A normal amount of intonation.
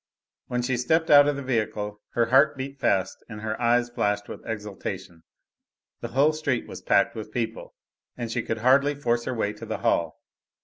Yes: average, 4.5 semitones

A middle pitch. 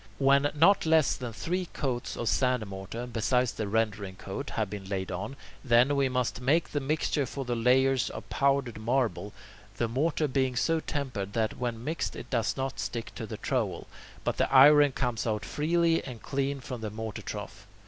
No: low, 125 Hz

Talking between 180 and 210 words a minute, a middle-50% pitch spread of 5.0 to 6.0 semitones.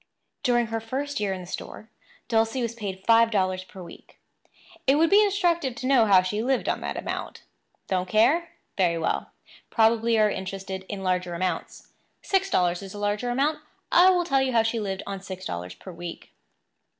Yes: average, 195 wpm; wide, 5.4 semitones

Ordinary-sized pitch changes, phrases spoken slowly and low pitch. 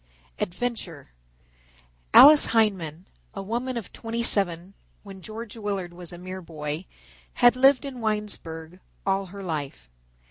No: average, 4.8 semitones; slow, 130 wpm; high, 195 Hz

